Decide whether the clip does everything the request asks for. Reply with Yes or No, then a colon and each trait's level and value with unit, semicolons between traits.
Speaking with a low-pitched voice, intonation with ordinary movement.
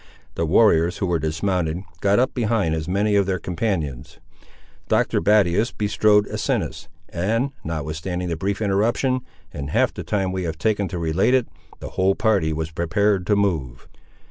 Yes: very low, 95 Hz; average, 4.2 semitones